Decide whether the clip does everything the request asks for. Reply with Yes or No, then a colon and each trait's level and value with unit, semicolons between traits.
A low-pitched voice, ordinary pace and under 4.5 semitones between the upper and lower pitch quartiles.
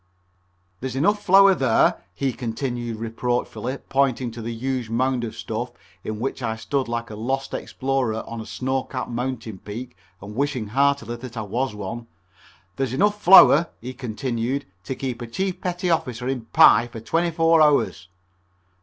Yes: low, 125 Hz; average, 165 wpm; average, 2.9 semitones